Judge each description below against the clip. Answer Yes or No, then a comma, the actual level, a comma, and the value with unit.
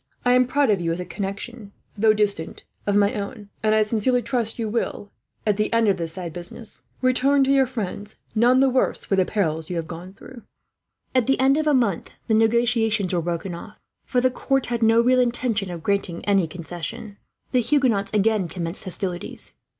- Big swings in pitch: No, average, 4.7 semitones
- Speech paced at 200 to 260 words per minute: Yes, fast, 205 wpm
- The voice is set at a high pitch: Yes, high, 215 Hz